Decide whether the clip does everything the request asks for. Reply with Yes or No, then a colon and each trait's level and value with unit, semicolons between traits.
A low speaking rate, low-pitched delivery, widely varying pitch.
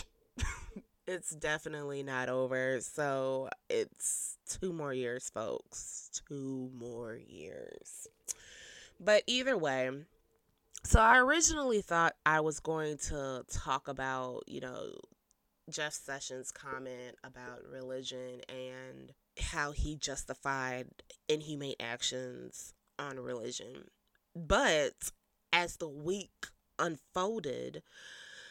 No: slow, 95 wpm; medium, 145 Hz; wide, 6.1 semitones